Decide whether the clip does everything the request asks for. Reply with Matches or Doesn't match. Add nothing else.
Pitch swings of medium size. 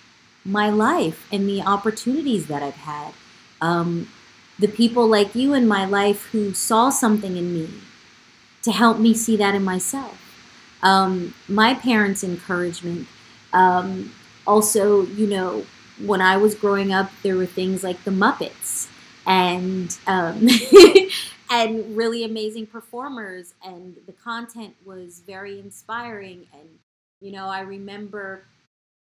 Matches